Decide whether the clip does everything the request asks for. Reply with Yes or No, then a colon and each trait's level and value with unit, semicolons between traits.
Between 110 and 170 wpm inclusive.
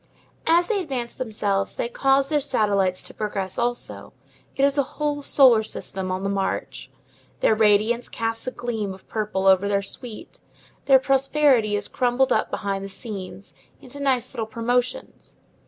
Yes: average, 160 wpm